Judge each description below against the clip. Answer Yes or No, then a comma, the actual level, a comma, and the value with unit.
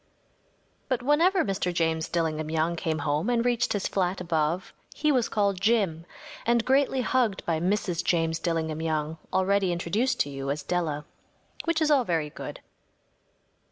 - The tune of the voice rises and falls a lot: Yes, wide, 6.5 semitones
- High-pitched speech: No, medium, 180 Hz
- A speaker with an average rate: Yes, average, 160 wpm